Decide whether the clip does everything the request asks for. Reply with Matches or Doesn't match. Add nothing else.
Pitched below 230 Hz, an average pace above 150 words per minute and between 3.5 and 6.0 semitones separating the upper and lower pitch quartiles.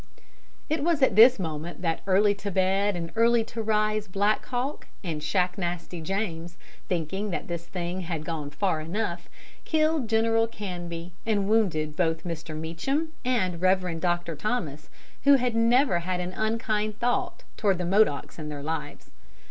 Matches